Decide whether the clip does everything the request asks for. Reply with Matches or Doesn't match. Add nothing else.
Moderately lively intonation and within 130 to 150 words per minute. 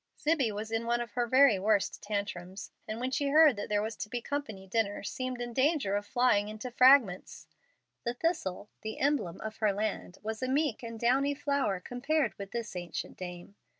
Doesn't match